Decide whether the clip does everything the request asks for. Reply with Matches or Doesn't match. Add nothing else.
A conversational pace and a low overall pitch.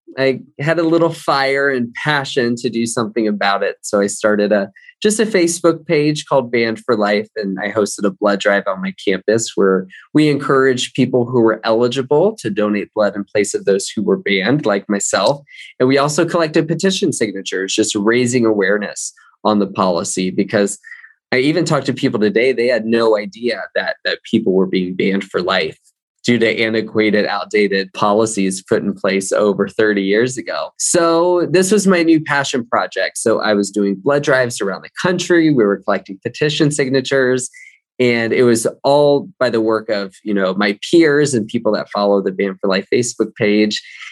Matches